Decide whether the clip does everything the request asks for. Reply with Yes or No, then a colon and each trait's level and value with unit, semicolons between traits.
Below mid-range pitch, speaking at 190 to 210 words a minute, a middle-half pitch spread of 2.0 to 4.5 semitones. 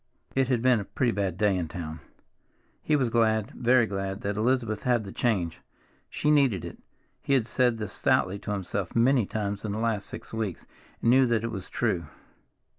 Yes: low, 110 Hz; average, 195 wpm; average, 3.7 semitones